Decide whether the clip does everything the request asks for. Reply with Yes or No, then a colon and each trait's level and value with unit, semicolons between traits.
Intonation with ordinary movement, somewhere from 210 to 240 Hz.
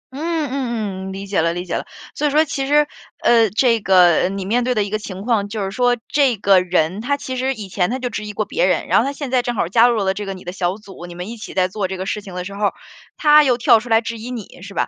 Yes: average, 4.5 semitones; high, 215 Hz